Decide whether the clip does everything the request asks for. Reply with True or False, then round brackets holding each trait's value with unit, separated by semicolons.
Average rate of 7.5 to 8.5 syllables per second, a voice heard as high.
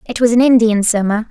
False (5.3 syllables/s; 225 Hz)